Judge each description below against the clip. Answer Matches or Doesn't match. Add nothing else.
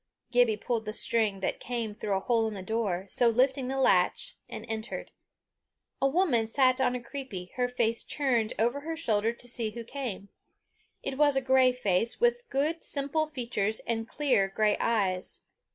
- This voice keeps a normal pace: Matches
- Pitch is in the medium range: Doesn't match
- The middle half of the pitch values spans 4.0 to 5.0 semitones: Doesn't match